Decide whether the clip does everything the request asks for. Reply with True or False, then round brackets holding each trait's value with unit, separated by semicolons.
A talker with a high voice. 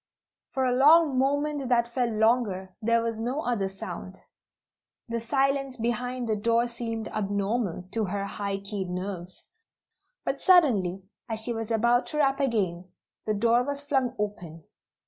True (230 Hz)